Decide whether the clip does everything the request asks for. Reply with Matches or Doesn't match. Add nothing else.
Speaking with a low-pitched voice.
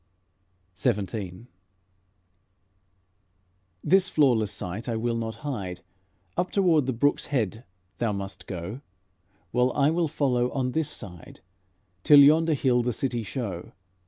Matches